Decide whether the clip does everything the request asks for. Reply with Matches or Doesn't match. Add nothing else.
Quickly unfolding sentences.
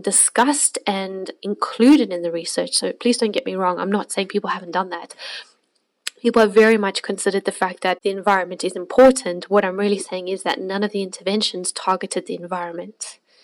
Doesn't match